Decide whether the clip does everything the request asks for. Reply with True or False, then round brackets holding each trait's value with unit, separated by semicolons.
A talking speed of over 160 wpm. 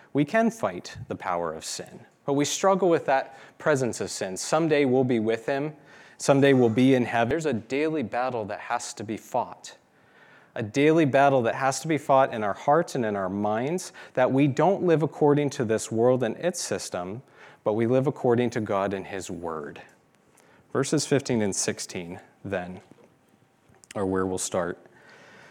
True (185 wpm)